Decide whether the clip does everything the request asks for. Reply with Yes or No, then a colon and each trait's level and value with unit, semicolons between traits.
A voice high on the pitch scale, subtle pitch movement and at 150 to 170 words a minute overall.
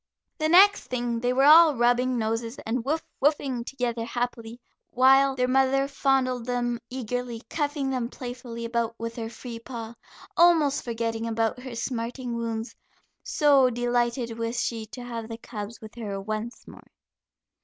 Yes: high, 245 Hz; narrow, 2.3 semitones; average, 155 wpm